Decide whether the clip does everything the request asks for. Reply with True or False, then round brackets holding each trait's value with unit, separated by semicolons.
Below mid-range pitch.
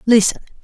False (220 Hz)